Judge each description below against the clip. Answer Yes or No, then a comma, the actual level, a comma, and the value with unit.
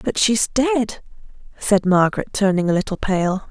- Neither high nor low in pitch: No, high, 195 Hz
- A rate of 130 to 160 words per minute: Yes, average, 155 wpm